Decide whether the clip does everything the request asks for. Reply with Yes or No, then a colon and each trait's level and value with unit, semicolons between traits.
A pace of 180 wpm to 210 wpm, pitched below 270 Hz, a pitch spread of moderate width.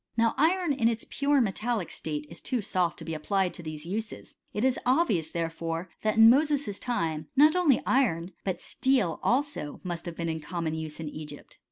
No: average, 200 wpm; high, 190 Hz; wide, 7.6 semitones